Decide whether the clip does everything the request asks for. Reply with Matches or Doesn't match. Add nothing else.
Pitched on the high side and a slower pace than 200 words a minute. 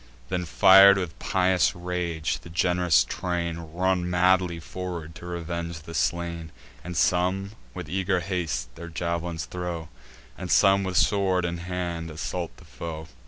Doesn't match